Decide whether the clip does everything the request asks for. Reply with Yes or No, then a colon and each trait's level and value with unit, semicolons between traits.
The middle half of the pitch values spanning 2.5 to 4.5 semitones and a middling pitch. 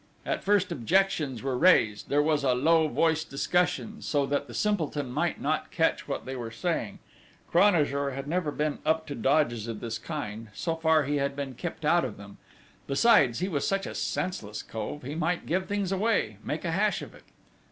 No: average, 4.9 semitones; medium, 150 Hz